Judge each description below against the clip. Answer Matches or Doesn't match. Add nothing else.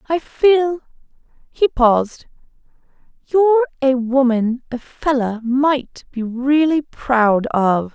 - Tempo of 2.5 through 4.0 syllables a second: Matches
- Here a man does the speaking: Doesn't match